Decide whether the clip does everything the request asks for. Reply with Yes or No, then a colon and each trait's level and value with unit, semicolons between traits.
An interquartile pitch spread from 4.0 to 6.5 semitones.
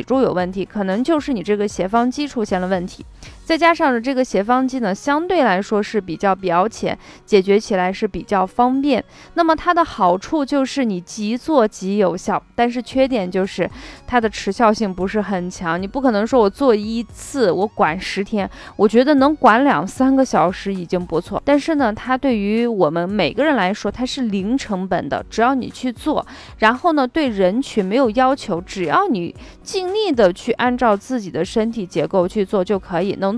Yes: wide, 5.4 semitones